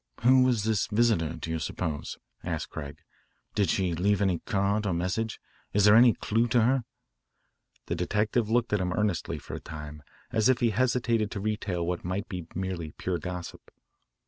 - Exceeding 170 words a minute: Yes, average, 180 wpm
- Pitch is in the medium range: No, low, 100 Hz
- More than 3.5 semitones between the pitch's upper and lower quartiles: Yes, average, 4.1 semitones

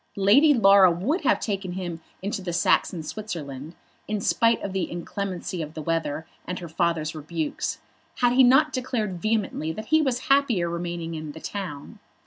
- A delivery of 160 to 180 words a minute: Yes, average, 170 wpm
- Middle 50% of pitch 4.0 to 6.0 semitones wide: Yes, average, 5.0 semitones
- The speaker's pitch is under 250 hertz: Yes, medium, 185 Hz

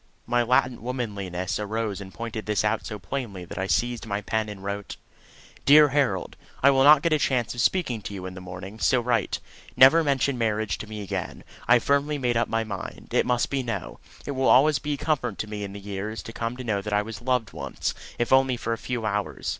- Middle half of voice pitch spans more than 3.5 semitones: Yes, average, 4.0 semitones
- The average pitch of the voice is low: Yes, low, 115 Hz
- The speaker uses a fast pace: Yes, fast, 235 wpm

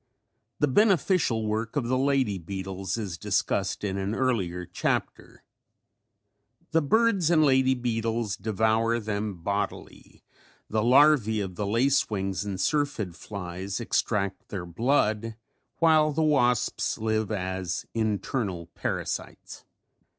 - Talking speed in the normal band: No, slow, 120 wpm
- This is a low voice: Yes, low, 110 Hz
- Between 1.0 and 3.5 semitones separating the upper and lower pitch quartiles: No, average, 5.2 semitones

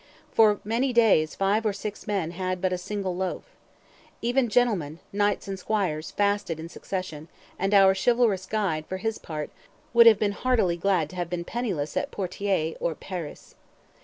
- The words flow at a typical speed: Yes, average, 170 wpm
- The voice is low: No, high, 195 Hz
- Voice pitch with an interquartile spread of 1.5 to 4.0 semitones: Yes, average, 3.4 semitones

